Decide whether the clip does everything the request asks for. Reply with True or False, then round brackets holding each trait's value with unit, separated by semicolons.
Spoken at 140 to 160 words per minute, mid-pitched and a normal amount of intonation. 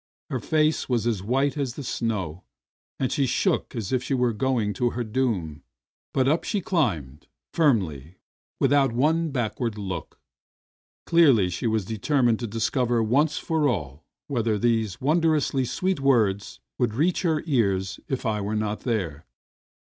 False (155 wpm; 120 Hz; 5.0 semitones)